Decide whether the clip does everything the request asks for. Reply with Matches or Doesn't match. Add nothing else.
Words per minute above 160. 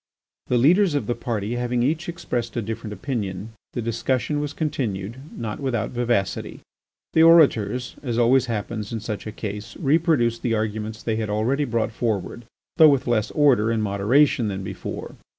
Matches